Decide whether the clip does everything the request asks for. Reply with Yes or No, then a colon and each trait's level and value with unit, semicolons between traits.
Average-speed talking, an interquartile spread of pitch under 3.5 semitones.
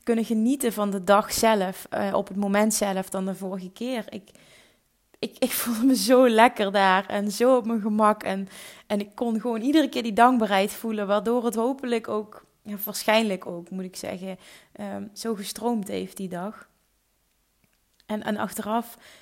Yes: average, 180 wpm; average, 2.7 semitones